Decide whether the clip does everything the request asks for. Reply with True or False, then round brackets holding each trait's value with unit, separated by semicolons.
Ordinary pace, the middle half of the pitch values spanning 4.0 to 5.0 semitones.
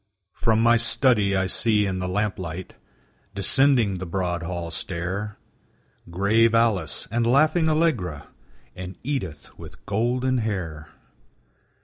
False (115 wpm; 4.4 semitones)